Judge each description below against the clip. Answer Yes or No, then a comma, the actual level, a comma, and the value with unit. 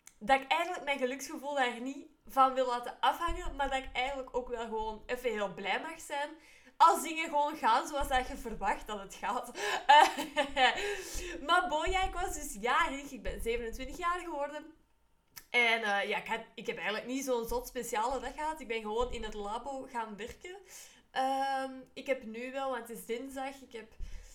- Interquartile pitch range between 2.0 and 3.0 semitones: No, average, 4.1 semitones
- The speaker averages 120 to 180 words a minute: No, average, 195 wpm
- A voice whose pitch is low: No, very high, 260 Hz